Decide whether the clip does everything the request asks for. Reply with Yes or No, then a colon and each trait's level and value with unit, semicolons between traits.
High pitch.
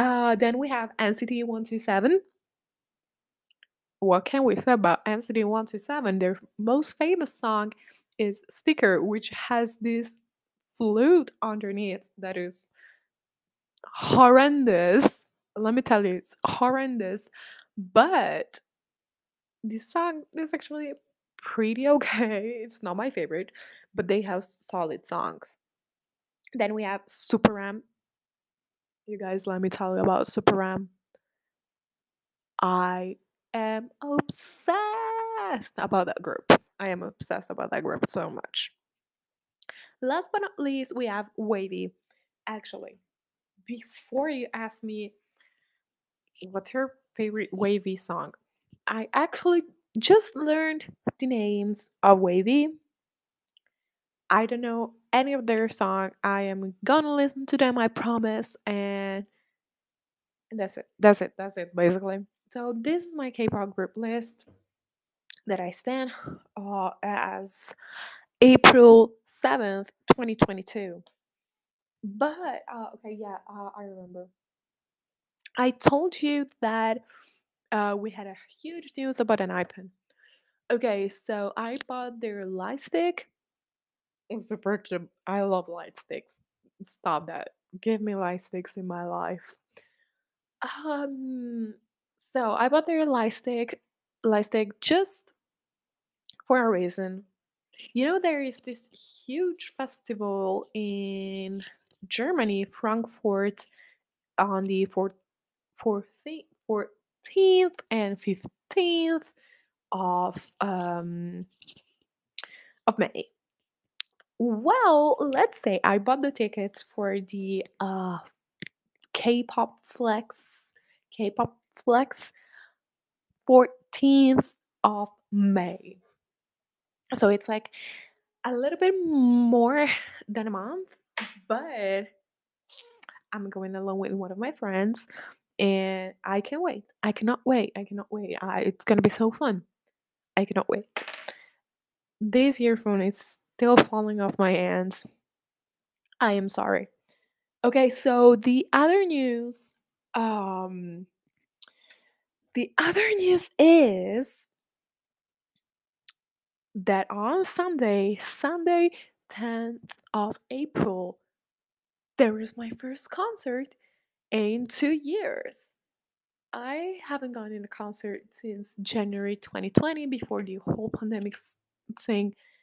Yes: high, 225 Hz